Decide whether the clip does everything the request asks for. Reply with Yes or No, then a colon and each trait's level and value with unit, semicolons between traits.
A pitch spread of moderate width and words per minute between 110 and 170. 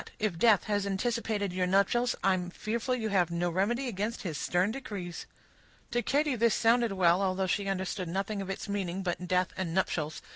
No: average, 3.5 semitones; average, 190 wpm